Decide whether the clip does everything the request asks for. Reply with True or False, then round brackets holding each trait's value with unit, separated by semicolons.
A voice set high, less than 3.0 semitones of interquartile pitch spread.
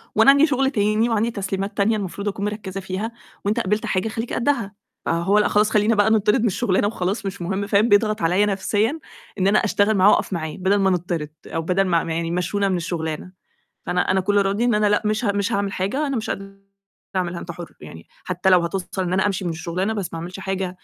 True (195 Hz; 2.6 semitones)